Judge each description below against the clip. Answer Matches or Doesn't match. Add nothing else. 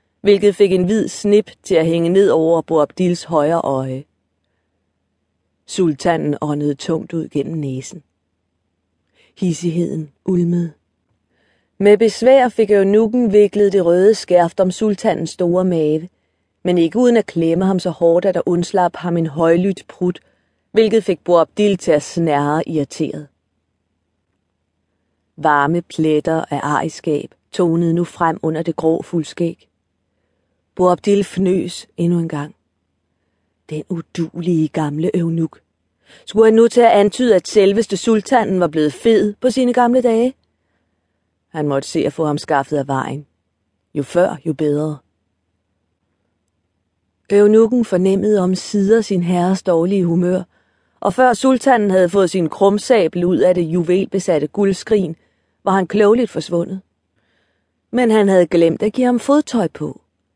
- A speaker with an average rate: Doesn't match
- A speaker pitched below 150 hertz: Doesn't match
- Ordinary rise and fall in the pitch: Doesn't match